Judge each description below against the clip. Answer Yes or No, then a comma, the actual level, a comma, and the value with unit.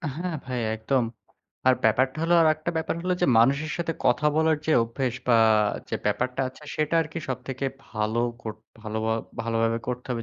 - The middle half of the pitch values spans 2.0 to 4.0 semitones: No, average, 5.2 semitones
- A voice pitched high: No, low, 130 Hz